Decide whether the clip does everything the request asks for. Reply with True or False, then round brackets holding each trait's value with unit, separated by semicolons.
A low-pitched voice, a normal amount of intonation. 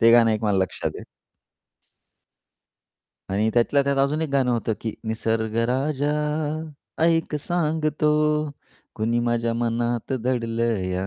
True (120 Hz; 4.3 semitones)